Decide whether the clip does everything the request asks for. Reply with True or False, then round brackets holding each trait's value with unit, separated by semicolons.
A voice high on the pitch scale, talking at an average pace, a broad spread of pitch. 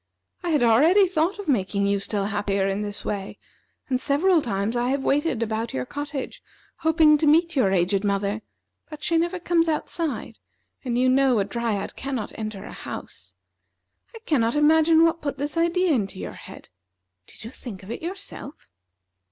True (270 Hz; 175 wpm; 7.5 semitones)